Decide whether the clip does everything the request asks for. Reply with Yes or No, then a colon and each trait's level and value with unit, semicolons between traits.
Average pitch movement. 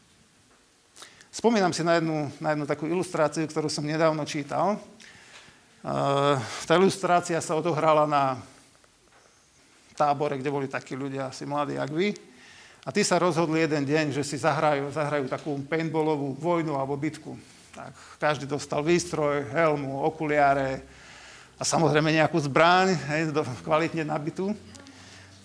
No: narrow, 2.3 semitones